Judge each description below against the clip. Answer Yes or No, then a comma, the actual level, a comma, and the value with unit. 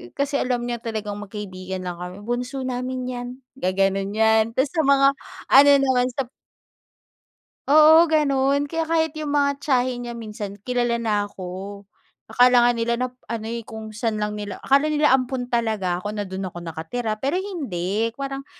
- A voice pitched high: Yes, high, 240 Hz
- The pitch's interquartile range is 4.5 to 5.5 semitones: Yes, average, 4.9 semitones